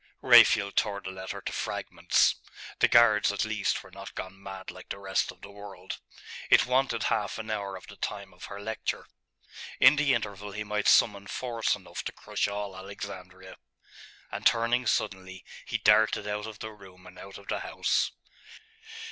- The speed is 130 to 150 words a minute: No, average, 180 wpm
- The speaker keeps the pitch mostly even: Yes, narrow, 2.1 semitones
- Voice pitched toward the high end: No, low, 100 Hz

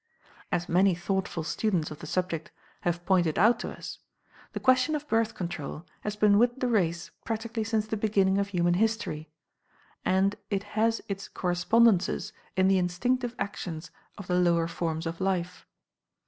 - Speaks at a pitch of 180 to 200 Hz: Yes, high, 190 Hz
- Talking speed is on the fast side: No, average, 160 wpm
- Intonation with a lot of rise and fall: No, average, 4.0 semitones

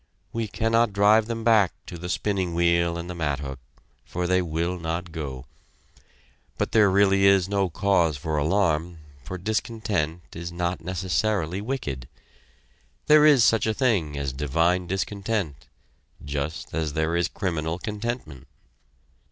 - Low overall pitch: Yes, very low, 90 Hz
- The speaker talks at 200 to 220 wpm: No, average, 140 wpm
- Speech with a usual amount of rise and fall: Yes, average, 4.3 semitones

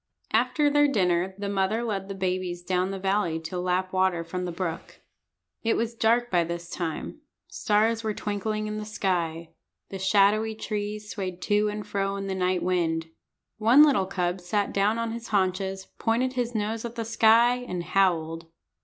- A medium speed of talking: Yes, average, 180 wpm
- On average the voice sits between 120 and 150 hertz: No, high, 195 Hz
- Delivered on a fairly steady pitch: No, average, 3.4 semitones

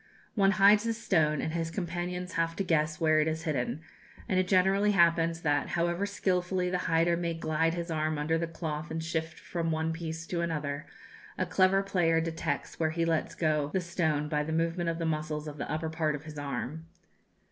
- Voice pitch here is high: No, medium, 165 Hz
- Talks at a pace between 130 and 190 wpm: No, fast, 205 wpm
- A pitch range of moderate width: No, narrow, 1.9 semitones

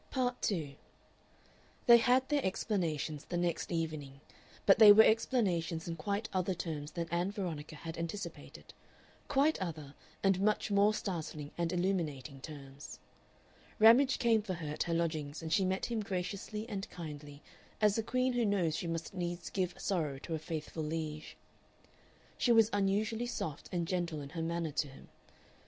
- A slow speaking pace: No, average, 165 wpm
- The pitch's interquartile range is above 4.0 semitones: Yes, average, 4.8 semitones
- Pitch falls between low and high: Yes, medium, 175 Hz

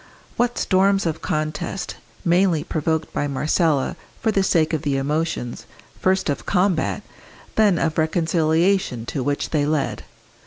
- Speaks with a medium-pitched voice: Yes, medium, 160 Hz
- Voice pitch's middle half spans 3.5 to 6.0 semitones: Yes, average, 3.8 semitones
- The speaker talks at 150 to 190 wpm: No, average, 140 wpm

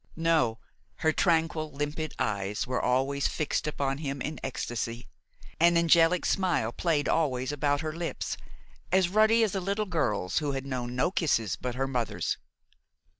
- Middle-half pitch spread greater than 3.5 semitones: Yes, average, 4.7 semitones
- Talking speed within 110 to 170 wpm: Yes, average, 155 wpm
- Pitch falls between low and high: Yes, medium, 145 Hz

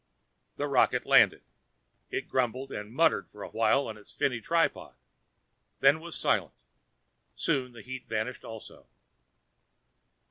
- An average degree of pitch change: Yes, average, 3.7 semitones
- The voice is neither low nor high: No, low, 125 Hz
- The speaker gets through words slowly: Yes, slow, 130 wpm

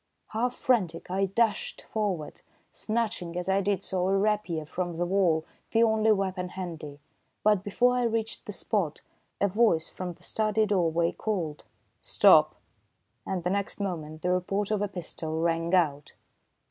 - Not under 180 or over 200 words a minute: No, average, 160 wpm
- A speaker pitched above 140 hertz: Yes, high, 190 Hz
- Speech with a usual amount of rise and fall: Yes, average, 3.8 semitones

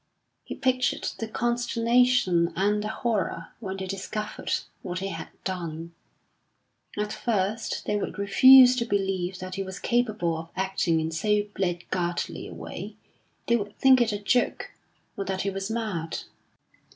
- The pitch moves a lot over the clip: No, average, 3.7 semitones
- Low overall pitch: No, high, 200 Hz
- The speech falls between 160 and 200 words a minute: No, average, 150 wpm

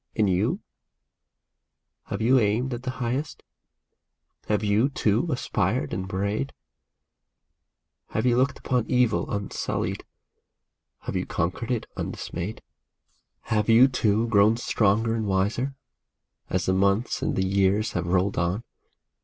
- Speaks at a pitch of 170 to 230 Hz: No, low, 110 Hz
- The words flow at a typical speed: No, slow, 130 wpm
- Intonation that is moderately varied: Yes, average, 3.8 semitones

